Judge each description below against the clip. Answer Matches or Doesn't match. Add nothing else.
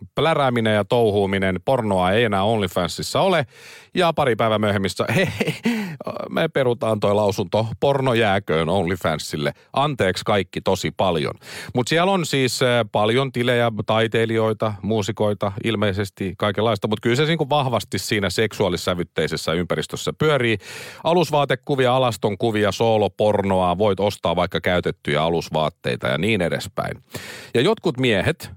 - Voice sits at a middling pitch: Doesn't match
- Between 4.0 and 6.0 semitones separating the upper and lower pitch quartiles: Doesn't match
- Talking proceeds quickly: Doesn't match